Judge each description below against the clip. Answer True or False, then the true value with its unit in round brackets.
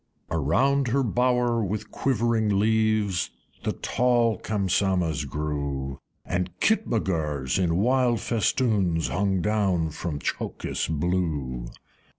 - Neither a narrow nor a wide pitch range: False (6.2 semitones)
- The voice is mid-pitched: False (95 Hz)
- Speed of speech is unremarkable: False (100 wpm)